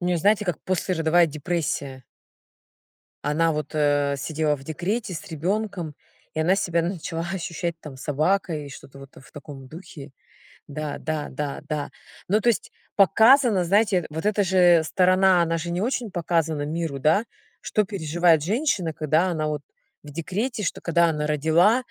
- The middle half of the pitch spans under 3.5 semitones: No, average, 3.8 semitones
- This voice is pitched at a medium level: Yes, medium, 165 Hz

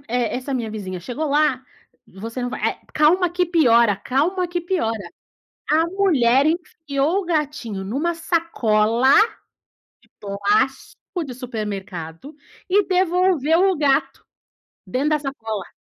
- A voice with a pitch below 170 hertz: No, very high, 280 Hz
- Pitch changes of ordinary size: No, wide, 6.7 semitones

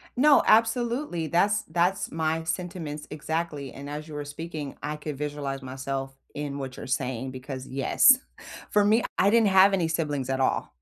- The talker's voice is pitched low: No, medium, 150 Hz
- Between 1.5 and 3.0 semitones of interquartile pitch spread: No, average, 5.0 semitones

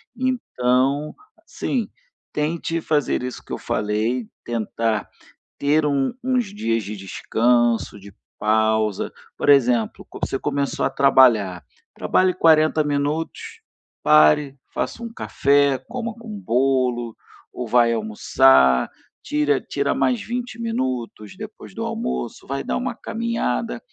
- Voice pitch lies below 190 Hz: Yes, low, 135 Hz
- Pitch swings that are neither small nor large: No, wide, 5.8 semitones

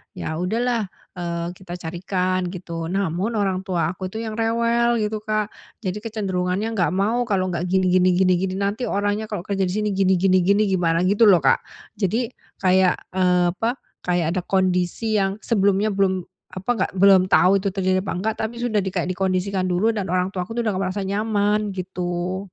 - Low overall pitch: No, high, 190 Hz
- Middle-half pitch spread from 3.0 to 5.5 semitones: No, narrow, 2.5 semitones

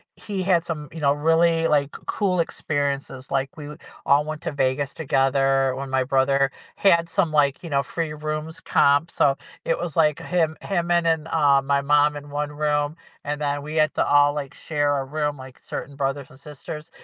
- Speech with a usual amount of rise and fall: No, narrow, 2.3 semitones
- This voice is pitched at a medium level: Yes, medium, 145 Hz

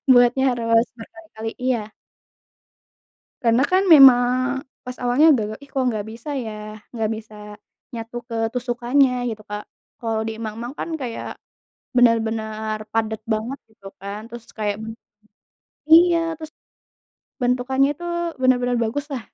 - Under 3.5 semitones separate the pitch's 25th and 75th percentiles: Yes, average, 3.1 semitones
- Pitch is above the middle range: Yes, high, 240 Hz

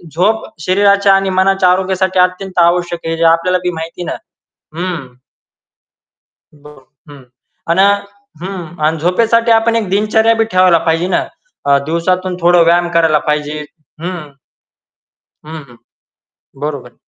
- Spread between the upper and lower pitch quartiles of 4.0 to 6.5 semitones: No, average, 2.8 semitones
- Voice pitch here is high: No, medium, 180 Hz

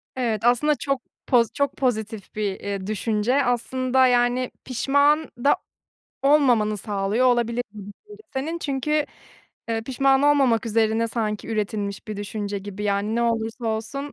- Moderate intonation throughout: Yes, average, 3.9 semitones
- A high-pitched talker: Yes, high, 235 Hz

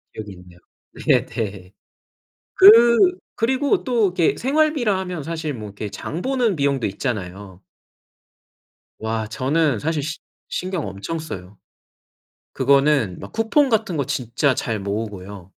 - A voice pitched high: No, medium, 140 Hz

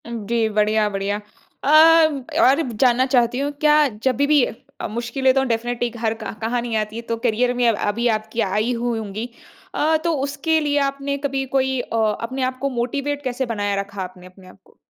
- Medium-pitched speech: No, high, 240 Hz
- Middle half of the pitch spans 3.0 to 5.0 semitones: Yes, average, 3.7 semitones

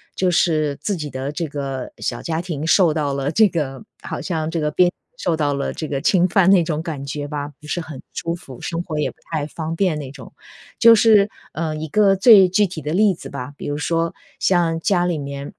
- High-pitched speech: No, medium, 160 Hz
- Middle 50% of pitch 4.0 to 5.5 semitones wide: No, average, 3.5 semitones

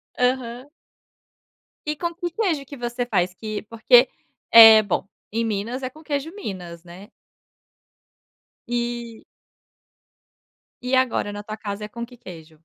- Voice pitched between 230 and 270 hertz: Yes, high, 235 Hz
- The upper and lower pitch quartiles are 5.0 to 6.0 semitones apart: No, average, 3.9 semitones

